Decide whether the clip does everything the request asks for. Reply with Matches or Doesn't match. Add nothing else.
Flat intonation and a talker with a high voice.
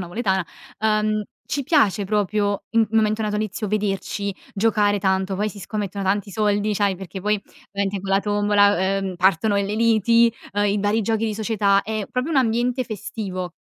Matches